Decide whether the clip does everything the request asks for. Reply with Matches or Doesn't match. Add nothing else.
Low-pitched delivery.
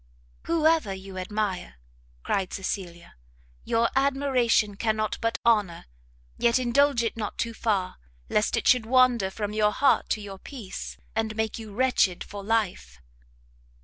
Doesn't match